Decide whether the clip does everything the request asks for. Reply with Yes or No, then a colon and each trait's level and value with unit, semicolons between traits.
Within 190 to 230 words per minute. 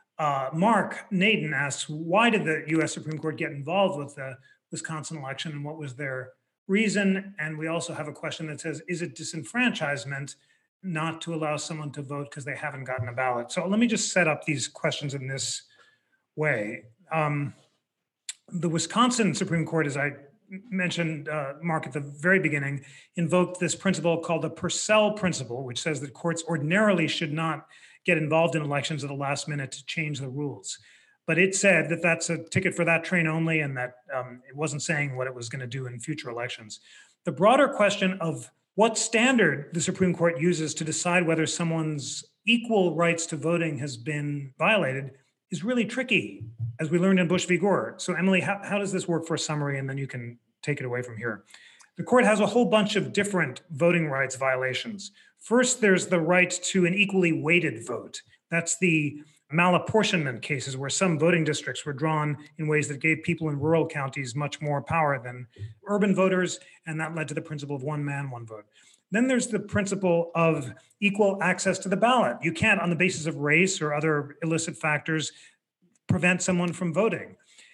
Yes: average, 195 wpm